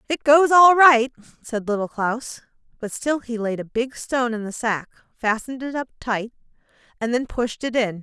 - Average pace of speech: Yes, average, 195 wpm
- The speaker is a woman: Yes, female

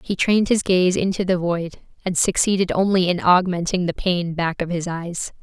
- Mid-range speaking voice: Yes, medium, 180 Hz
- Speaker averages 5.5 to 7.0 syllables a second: No, 5.0 syllables/s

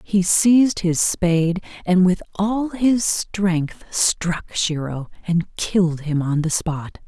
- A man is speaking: No, female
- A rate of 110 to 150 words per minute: Yes, average, 145 wpm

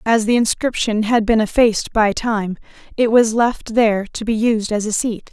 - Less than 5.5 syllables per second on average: Yes, 4.8 syllables/s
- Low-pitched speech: No, high, 220 Hz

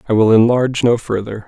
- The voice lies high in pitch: No, low, 115 Hz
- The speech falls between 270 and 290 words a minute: No, fast, 205 wpm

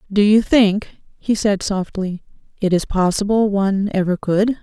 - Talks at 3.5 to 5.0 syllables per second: Yes, 4.5 syllables/s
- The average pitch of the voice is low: No, high, 200 Hz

